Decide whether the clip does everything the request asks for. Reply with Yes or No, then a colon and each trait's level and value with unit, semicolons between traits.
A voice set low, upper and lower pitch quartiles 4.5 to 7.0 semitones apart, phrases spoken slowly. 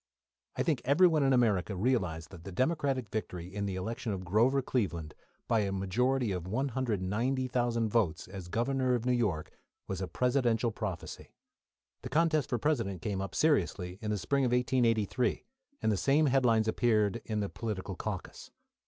No: low, 115 Hz; average, 4.9 semitones; average, 165 wpm